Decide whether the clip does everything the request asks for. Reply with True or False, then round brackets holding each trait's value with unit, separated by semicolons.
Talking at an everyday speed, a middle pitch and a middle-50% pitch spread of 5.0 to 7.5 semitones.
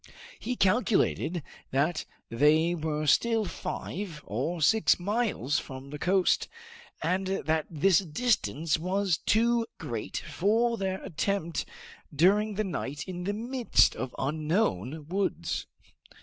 False (120 wpm; 175 Hz; 5.3 semitones)